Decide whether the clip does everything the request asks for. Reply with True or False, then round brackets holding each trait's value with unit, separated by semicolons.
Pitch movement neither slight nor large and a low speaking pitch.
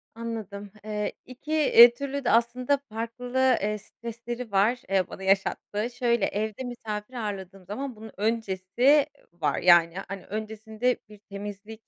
False (3.3 semitones; 220 Hz)